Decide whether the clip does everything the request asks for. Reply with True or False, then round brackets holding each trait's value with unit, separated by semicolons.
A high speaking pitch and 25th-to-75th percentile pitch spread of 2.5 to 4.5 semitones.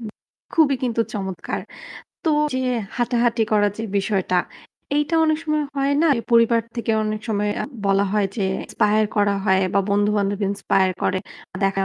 True (215 Hz; 3.3 semitones)